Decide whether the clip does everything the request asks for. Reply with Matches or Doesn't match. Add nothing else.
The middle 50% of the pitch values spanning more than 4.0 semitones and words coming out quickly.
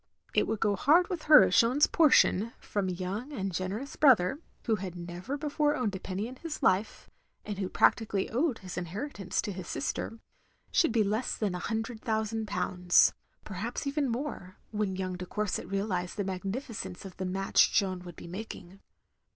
Doesn't match